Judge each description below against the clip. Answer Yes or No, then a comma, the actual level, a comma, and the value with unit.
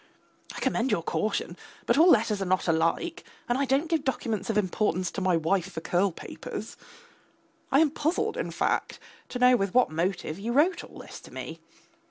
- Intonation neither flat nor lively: No, wide, 6.7 semitones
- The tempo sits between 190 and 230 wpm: Yes, average, 195 wpm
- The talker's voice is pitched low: No, high, 215 Hz